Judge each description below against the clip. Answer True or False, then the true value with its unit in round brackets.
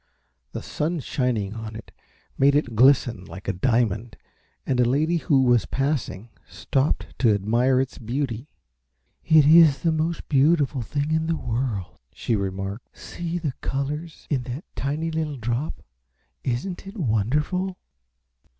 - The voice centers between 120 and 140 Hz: True (135 Hz)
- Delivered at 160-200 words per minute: False (140 wpm)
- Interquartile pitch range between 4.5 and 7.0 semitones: True (5.2 semitones)